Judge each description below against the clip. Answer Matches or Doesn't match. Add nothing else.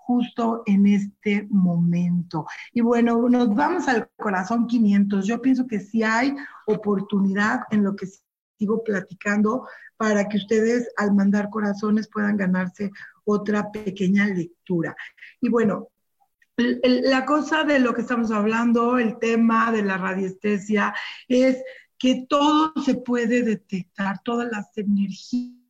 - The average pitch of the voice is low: Doesn't match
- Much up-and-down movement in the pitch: Doesn't match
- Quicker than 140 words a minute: Doesn't match